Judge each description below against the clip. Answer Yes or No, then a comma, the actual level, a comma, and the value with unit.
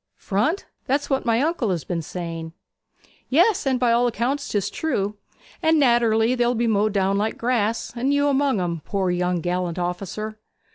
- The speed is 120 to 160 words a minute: No, average, 175 wpm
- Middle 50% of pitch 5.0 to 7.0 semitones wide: Yes, wide, 5.5 semitones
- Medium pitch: No, high, 225 Hz